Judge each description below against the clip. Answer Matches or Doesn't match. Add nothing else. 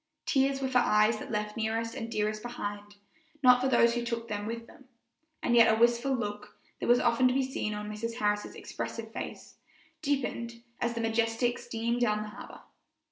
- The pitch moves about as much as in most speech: Doesn't match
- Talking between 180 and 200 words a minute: Matches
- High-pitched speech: Matches